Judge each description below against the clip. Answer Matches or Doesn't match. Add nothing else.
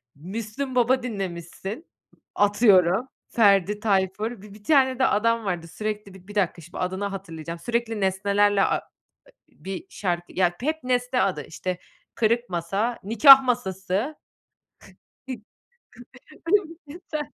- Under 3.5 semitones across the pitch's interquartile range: Doesn't match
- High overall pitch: Matches